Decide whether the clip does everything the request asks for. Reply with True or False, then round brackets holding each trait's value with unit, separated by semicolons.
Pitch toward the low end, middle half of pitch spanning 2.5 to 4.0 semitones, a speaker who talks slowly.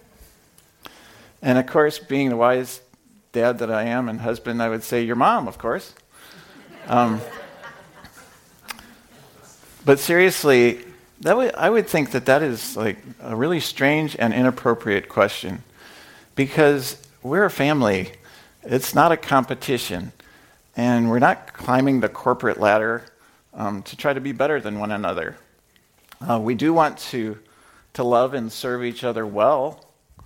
False (125 Hz; 3.4 semitones; 145 wpm)